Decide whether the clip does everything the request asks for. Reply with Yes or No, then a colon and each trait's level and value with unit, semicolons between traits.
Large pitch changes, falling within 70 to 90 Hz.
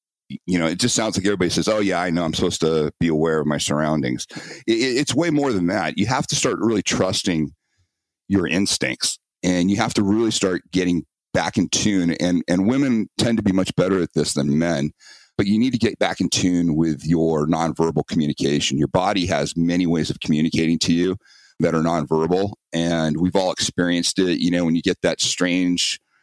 No: narrow, 2.5 semitones; very low, 85 Hz